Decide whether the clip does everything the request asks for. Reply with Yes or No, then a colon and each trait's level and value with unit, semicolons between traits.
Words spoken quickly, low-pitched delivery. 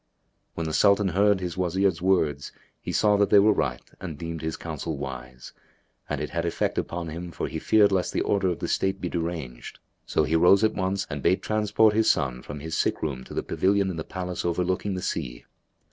Yes: fast, 220 wpm; very low, 90 Hz